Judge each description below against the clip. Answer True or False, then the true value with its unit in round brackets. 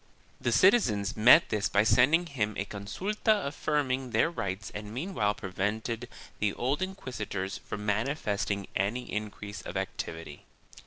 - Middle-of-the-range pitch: False (110 Hz)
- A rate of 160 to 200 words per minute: False (145 wpm)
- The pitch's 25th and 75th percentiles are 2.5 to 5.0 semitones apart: False (5.5 semitones)